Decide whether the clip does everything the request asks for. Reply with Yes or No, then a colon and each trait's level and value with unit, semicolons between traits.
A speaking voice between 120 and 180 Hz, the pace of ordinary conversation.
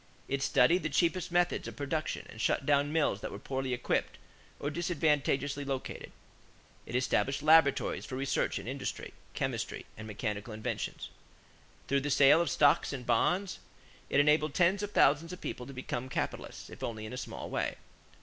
Yes: medium, 140 Hz; average, 170 wpm